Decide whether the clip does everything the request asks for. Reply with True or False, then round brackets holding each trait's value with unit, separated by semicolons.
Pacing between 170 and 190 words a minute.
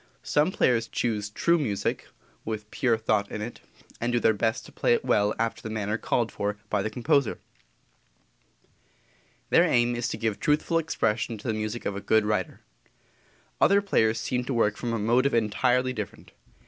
True (180 wpm)